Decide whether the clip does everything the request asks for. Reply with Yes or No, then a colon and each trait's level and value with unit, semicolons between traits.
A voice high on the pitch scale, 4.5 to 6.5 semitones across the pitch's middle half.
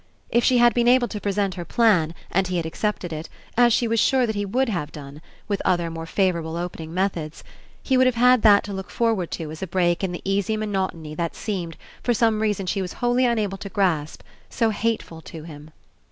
Yes: high, 195 Hz; average, 5.0 semitones